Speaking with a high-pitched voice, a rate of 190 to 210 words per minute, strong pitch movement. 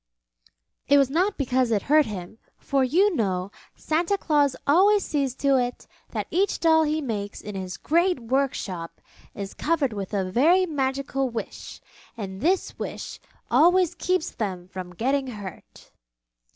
No: very high, 270 Hz; average, 150 wpm; wide, 7.4 semitones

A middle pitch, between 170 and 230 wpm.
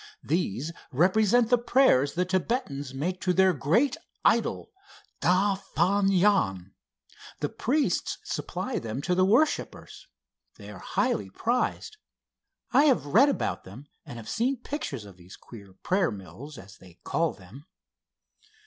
No: medium, 180 Hz; average, 140 wpm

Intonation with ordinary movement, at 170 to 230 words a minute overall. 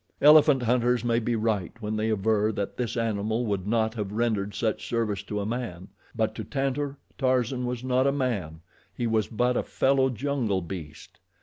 Yes: average, 3.3 semitones; average, 185 wpm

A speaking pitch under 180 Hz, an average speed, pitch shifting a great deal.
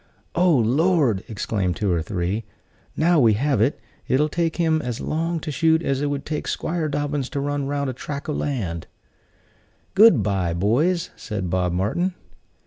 Yes: medium, 140 Hz; average, 170 wpm; wide, 7.1 semitones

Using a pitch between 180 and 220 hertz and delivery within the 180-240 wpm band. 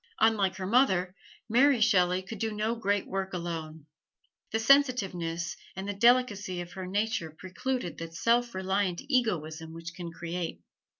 No: high, 190 Hz; average, 145 wpm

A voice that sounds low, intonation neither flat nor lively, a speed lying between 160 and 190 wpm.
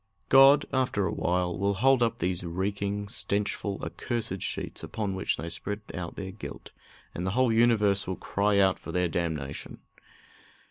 Yes: low, 100 Hz; average, 3.3 semitones; average, 165 wpm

